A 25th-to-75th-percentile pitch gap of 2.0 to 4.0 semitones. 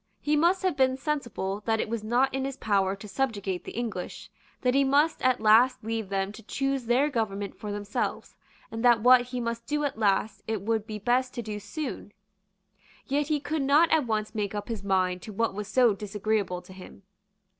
No: average, 4.5 semitones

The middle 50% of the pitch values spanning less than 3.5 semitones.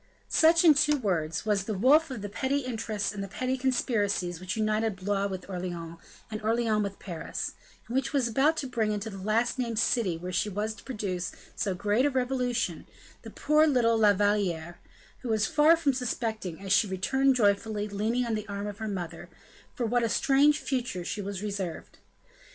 No: average, 4.2 semitones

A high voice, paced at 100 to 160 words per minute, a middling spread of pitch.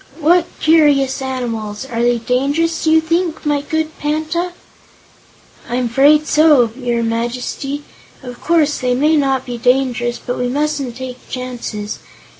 Yes: very high, 270 Hz; average, 140 wpm; average, 3.8 semitones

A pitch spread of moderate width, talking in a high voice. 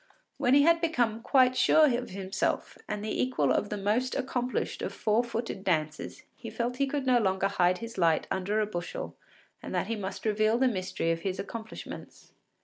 Yes: average, 4.6 semitones; high, 220 Hz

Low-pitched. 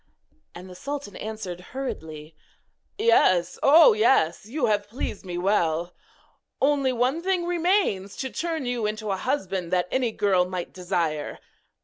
No: high, 210 Hz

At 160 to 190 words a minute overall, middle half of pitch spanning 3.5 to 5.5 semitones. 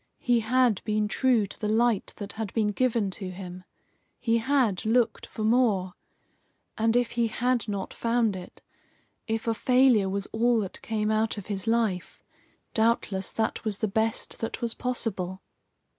No: average, 165 wpm; average, 2.7 semitones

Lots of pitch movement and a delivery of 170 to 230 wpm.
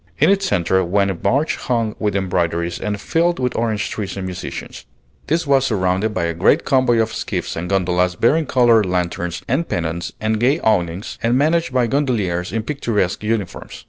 Yes: wide, 6.1 semitones; average, 180 wpm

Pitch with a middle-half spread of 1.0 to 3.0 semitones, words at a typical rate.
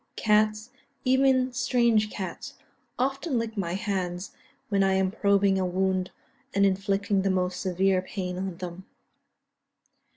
No: average, 2.7 semitones; slow, 130 wpm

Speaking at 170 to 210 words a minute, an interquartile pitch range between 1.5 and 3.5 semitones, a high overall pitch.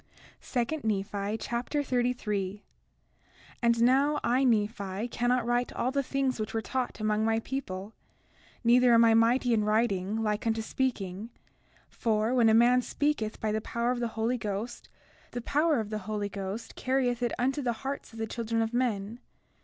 Yes: average, 175 wpm; narrow, 2.6 semitones; high, 230 Hz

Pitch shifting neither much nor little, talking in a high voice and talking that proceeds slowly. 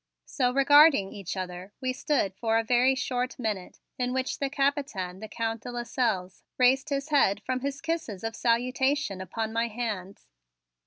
No: average, 4.6 semitones; high, 245 Hz; average, 165 wpm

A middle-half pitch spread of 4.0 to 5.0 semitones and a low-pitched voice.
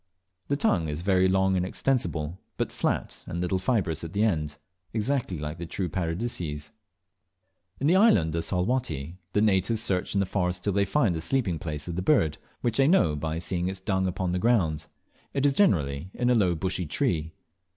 Yes: average, 4.7 semitones; very low, 90 Hz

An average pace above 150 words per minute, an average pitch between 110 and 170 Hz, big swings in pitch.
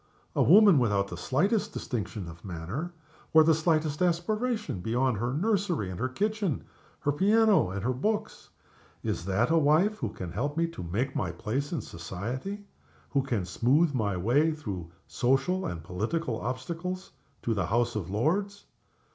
Yes: average, 165 wpm; low, 135 Hz; wide, 9.0 semitones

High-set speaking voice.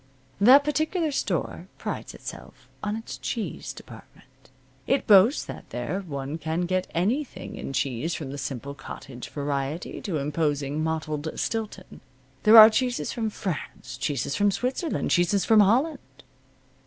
No: medium, 180 Hz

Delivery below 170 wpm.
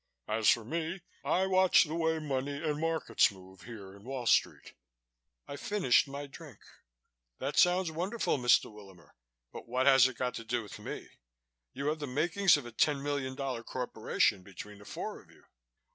No: average, 180 wpm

